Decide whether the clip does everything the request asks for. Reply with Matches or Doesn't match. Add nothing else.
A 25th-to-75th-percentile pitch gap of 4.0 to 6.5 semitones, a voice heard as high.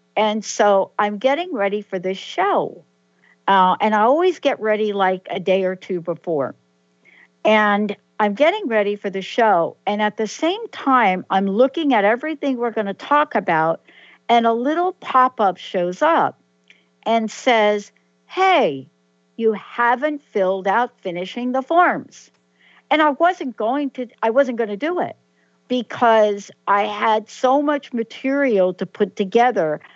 Matches